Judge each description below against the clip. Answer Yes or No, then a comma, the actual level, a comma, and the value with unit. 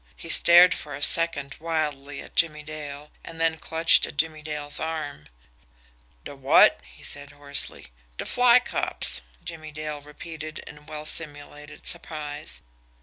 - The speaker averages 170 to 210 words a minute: No, average, 145 wpm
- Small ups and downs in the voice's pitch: Yes, narrow, 1.9 semitones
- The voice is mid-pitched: Yes, medium, 150 Hz